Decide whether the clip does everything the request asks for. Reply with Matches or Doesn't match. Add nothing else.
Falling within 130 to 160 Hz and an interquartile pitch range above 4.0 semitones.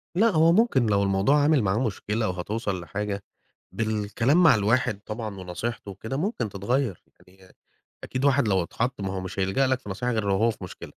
Doesn't match